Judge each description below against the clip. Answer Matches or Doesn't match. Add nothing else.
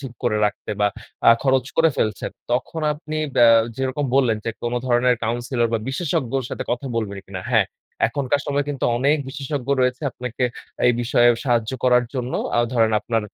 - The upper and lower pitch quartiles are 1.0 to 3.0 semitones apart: Matches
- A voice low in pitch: Matches